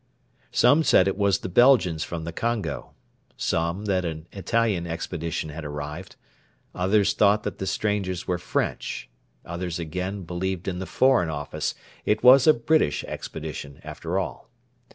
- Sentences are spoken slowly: No, average, 150 wpm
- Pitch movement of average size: Yes, average, 3.8 semitones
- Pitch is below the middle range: Yes, very low, 90 Hz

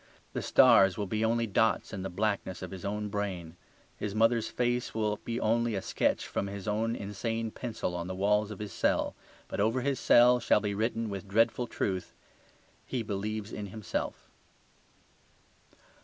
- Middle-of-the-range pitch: No, low, 105 Hz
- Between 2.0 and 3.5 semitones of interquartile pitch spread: Yes, narrow, 2.4 semitones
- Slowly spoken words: No, average, 170 wpm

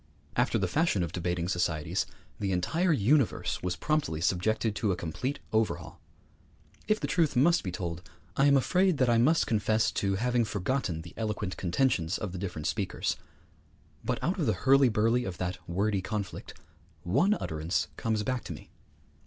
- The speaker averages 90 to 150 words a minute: No, average, 170 wpm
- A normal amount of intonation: No, wide, 6.8 semitones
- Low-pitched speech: Yes, low, 105 Hz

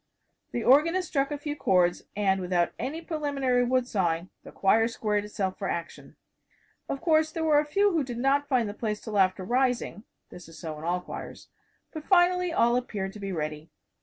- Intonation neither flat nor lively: No, wide, 7.4 semitones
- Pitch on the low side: No, high, 240 Hz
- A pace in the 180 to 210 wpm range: Yes, average, 195 wpm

